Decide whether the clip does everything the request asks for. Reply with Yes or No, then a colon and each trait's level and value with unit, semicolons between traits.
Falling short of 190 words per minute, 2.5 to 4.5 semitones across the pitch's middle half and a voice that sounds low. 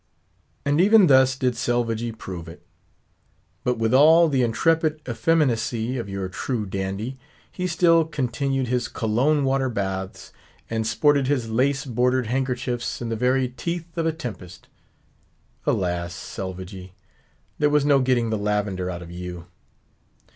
No: average, 140 wpm; average, 5.2 semitones; low, 125 Hz